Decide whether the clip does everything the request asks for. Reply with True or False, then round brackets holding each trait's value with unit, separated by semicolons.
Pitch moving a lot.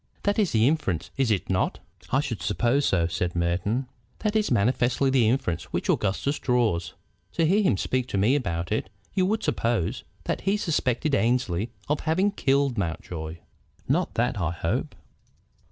True (7.2 semitones)